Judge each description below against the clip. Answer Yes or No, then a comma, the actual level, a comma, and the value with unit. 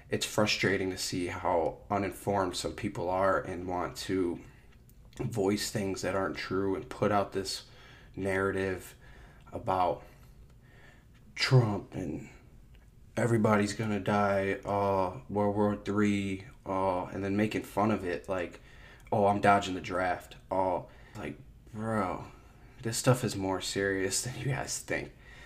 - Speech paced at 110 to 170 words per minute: Yes, slow, 135 wpm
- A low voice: Yes, low, 100 Hz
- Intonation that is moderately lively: Yes, average, 3.7 semitones